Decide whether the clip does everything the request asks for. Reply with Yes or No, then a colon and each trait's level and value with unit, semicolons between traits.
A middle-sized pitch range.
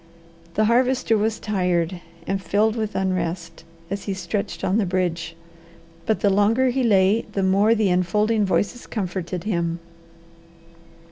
Yes: average, 3.2 semitones